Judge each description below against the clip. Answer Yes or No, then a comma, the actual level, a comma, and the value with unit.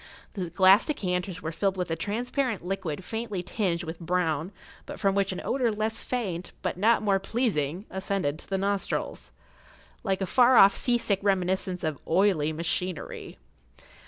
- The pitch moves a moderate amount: Yes, average, 3.0 semitones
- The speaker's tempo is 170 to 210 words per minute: No, average, 160 wpm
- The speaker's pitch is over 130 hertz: Yes, high, 190 Hz